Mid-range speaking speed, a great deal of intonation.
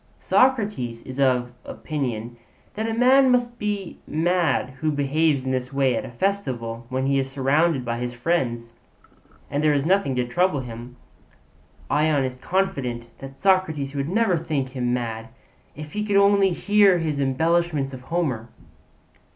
Yes: average, 160 wpm; wide, 6.2 semitones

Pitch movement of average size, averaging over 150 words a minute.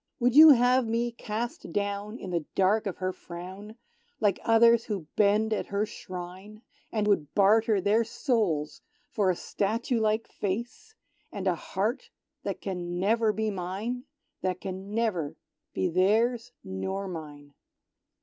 No: average, 3.5 semitones; average, 145 wpm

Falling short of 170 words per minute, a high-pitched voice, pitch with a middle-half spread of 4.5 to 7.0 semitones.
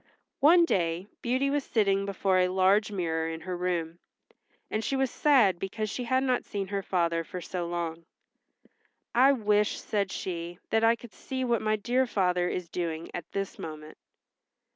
No: average, 175 wpm; high, 195 Hz; average, 5.0 semitones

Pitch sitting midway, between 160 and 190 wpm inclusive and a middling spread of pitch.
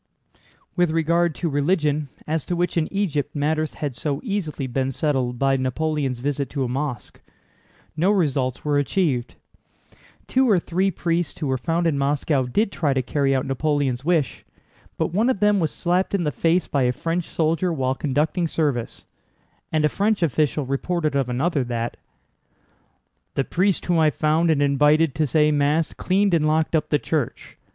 Yes: medium, 150 Hz; average, 175 wpm; average, 3.6 semitones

